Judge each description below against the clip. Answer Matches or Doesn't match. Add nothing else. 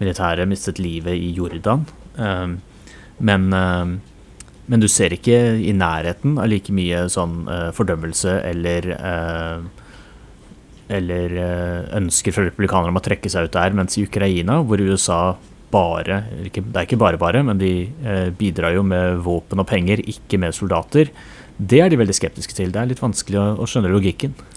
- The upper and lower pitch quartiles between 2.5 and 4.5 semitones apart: Matches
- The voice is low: Matches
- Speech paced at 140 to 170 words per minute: Matches